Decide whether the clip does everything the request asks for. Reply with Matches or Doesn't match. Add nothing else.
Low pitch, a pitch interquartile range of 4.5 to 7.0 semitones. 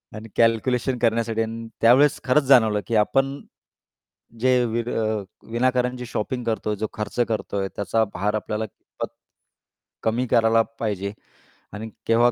Doesn't match